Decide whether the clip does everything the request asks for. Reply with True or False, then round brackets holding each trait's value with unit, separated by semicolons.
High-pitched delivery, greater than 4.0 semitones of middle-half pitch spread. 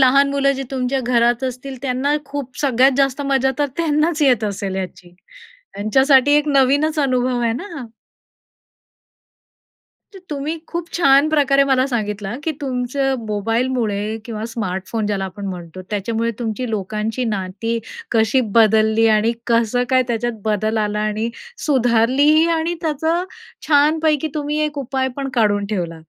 True (250 Hz; 4.4 semitones)